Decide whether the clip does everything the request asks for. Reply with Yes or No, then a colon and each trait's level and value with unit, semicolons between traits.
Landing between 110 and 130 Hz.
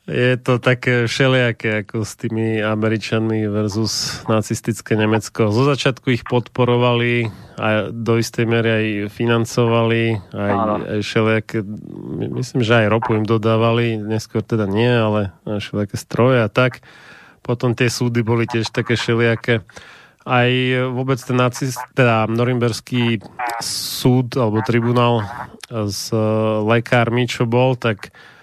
Yes: low, 115 Hz